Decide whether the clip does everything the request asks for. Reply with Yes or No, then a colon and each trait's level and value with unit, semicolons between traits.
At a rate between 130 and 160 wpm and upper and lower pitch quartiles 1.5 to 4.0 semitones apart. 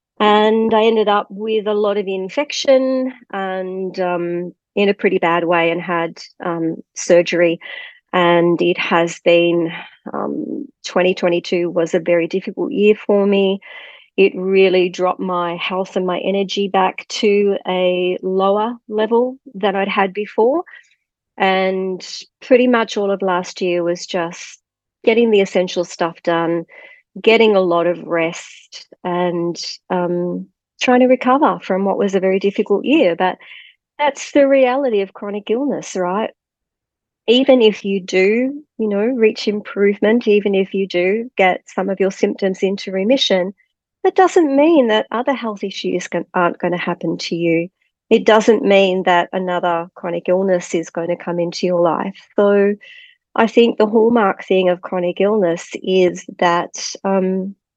Yes: average, 155 wpm; average, 3.6 semitones